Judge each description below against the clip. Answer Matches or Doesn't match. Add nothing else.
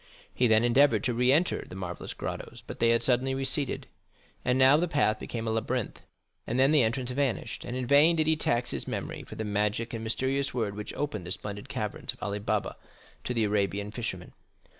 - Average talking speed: Doesn't match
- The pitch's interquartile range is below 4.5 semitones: Matches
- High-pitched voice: Doesn't match